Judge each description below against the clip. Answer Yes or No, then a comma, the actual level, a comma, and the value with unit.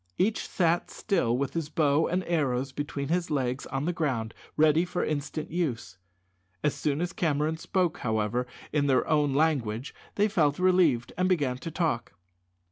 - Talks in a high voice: No, medium, 150 Hz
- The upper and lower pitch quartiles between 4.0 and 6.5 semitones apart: Yes, average, 4.4 semitones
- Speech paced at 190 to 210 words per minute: No, average, 165 wpm